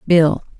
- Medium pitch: Yes, medium, 165 Hz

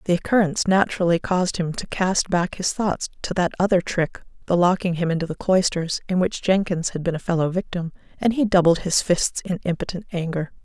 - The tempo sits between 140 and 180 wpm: No, average, 195 wpm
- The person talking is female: Yes, female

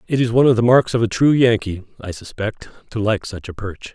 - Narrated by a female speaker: No, male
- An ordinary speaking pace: No, fast, 260 wpm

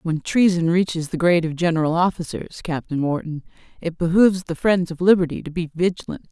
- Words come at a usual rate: Yes, average, 180 wpm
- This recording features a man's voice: No, female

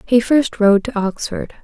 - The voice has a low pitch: No, high, 225 Hz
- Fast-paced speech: No, average, 185 wpm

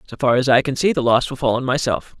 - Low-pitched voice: Yes, low, 130 Hz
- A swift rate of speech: Yes, fast, 325 wpm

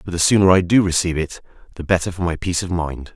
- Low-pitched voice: Yes, very low, 90 Hz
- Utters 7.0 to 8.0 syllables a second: Yes, 7.1 syllables/s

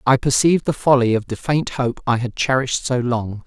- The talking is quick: Yes, fast, 225 wpm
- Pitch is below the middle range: Yes, low, 125 Hz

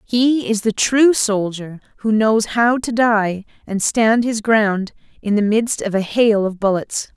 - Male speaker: No, female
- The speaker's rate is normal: Yes, average, 185 wpm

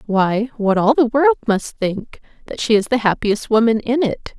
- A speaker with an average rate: Yes, average, 190 wpm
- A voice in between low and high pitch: No, high, 225 Hz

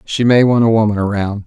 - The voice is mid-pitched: No, low, 110 Hz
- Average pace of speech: No, fast, 245 wpm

